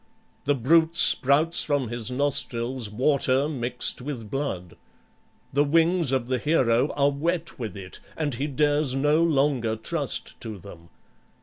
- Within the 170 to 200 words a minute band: No, average, 140 wpm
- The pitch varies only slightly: No, average, 4.0 semitones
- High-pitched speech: No, low, 135 Hz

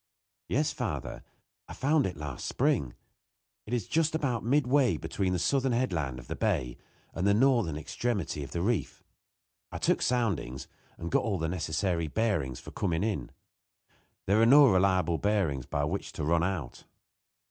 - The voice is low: Yes, very low, 95 Hz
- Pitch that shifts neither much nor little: No, wide, 7.1 semitones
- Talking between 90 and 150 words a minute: No, average, 165 wpm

